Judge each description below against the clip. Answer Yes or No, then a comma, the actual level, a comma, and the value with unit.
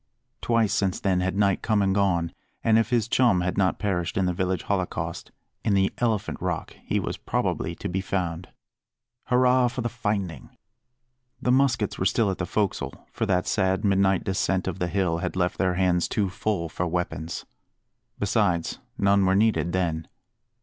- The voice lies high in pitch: No, very low, 95 Hz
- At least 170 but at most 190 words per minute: Yes, average, 175 wpm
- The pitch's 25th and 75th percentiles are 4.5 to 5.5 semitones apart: No, average, 2.8 semitones